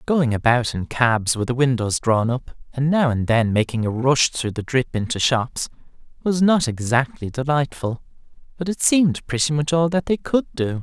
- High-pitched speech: No, low, 130 Hz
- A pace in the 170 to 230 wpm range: Yes, average, 195 wpm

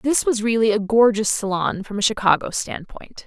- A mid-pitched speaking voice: No, high, 215 Hz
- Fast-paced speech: No, average, 185 wpm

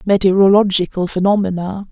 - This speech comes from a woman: Yes, female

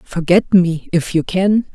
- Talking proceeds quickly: No, average, 170 wpm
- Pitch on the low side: No, medium, 180 Hz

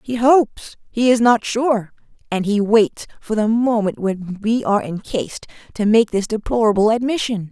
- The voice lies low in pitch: No, high, 220 Hz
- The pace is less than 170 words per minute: Yes, average, 160 wpm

